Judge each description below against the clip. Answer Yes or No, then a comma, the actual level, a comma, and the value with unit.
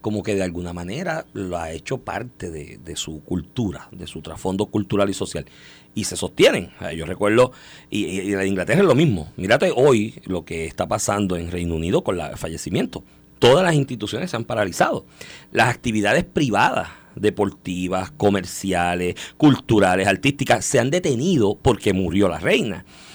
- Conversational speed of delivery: Yes, average, 165 wpm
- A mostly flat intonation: No, average, 3.2 semitones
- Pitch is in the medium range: No, low, 100 Hz